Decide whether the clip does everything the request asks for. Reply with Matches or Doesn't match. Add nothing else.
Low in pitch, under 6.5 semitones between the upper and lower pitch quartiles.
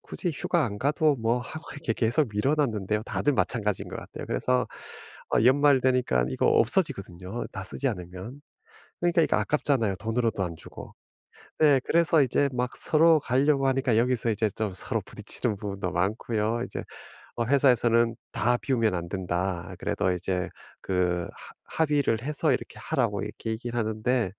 Matches